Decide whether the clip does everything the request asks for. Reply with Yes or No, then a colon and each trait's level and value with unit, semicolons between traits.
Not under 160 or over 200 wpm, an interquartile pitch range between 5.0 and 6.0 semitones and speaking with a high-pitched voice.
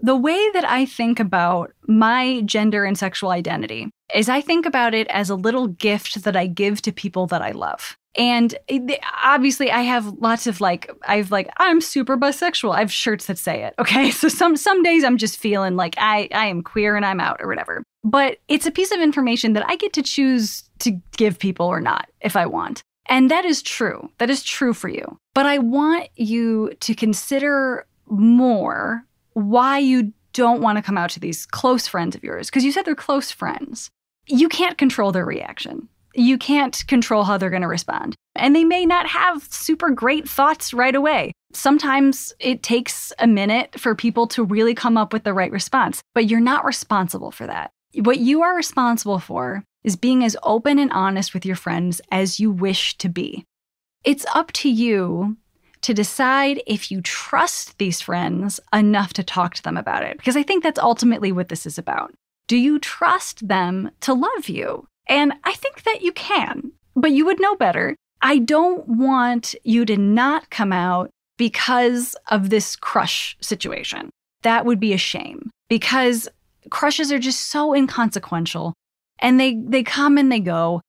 Yes: average, 190 wpm; average, 5.3 semitones; high, 235 Hz